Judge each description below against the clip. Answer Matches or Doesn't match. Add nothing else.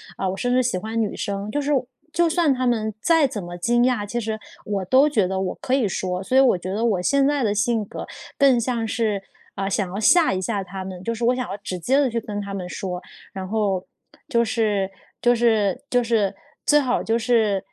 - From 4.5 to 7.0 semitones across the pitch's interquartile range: Doesn't match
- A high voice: Matches